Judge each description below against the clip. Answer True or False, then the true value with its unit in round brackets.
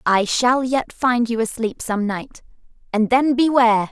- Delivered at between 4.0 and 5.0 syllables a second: True (4.2 syllables/s)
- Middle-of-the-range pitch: False (235 Hz)